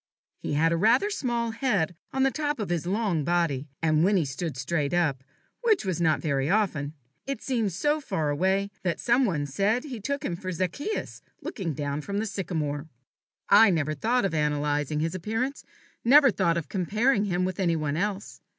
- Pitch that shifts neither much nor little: No, wide, 6.6 semitones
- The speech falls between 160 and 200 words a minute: Yes, average, 190 wpm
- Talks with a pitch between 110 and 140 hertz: No, medium, 185 Hz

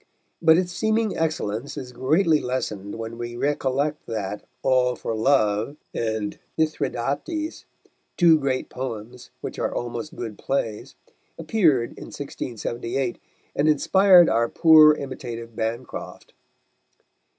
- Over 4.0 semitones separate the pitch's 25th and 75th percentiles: Yes, average, 5.0 semitones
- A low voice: Yes, low, 130 Hz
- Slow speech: Yes, slow, 115 wpm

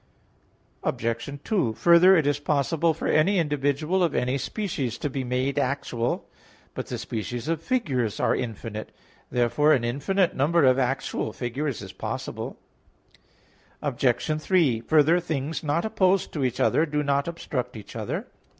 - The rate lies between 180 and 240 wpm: No, average, 150 wpm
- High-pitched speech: No, medium, 140 Hz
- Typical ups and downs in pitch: Yes, average, 4.7 semitones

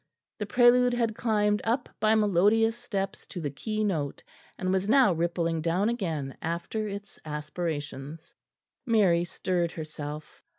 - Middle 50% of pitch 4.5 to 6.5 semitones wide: Yes, average, 5.0 semitones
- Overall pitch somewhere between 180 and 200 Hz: Yes, high, 190 Hz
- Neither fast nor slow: No, slow, 130 wpm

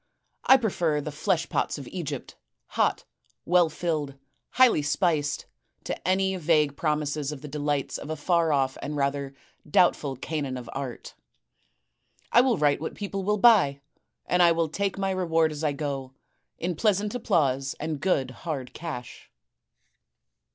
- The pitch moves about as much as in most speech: Yes, average, 4.1 semitones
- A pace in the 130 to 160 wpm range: Yes, average, 150 wpm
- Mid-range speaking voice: Yes, medium, 155 Hz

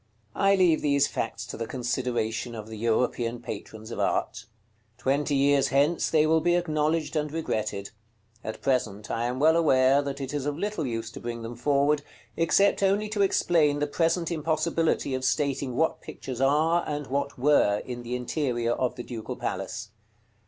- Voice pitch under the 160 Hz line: Yes, medium, 140 Hz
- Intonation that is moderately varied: Yes, average, 4.6 semitones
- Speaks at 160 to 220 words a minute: Yes, average, 180 wpm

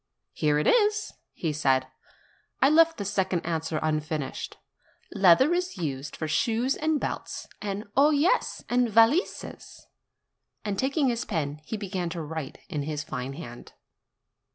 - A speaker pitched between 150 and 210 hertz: Yes, high, 190 Hz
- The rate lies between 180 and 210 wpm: No, average, 145 wpm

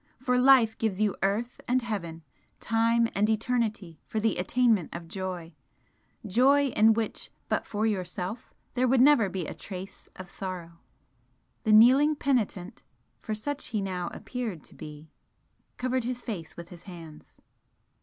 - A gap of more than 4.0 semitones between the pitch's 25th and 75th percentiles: Yes, average, 5.1 semitones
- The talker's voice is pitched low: No, high, 215 Hz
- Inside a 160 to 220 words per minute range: No, average, 150 wpm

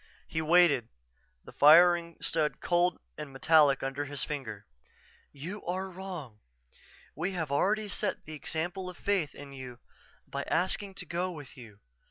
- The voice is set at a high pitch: No, medium, 160 Hz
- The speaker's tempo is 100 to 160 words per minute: Yes, average, 155 wpm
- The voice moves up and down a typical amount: Yes, average, 4.3 semitones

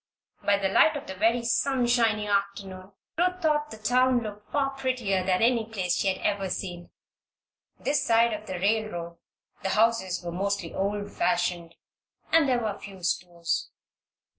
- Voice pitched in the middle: No, high, 205 Hz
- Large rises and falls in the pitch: No, average, 4.2 semitones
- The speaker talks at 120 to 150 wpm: No, average, 160 wpm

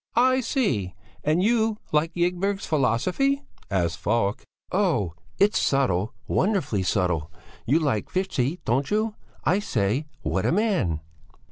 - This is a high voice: No, medium, 155 Hz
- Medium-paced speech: No, slow, 125 wpm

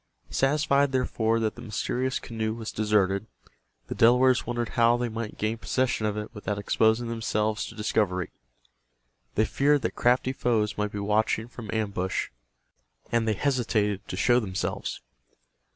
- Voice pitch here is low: Yes, low, 110 Hz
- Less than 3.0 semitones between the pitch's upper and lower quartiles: Yes, narrow, 2.4 semitones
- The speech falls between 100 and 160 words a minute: Yes, average, 150 wpm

